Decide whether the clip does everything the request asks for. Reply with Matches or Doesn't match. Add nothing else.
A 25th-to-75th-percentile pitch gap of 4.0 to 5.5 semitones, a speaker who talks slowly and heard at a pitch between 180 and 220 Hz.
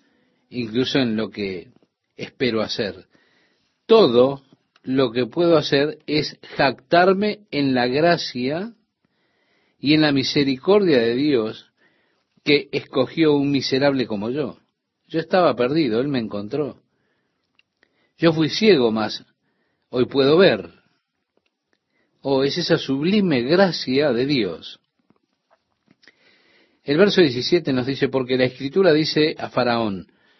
Doesn't match